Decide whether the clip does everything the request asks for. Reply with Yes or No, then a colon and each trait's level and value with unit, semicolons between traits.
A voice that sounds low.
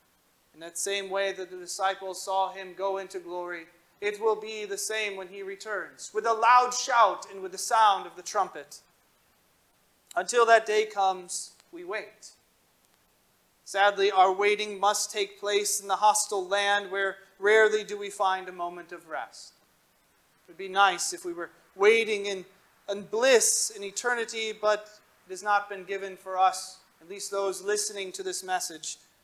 No: high, 200 Hz